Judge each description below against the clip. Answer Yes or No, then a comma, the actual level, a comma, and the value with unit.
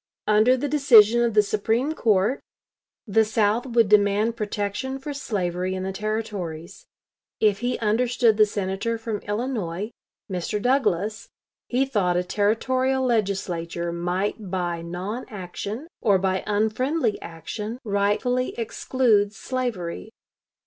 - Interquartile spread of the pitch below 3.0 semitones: No, average, 3.8 semitones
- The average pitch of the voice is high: Yes, high, 210 Hz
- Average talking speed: No, slow, 120 wpm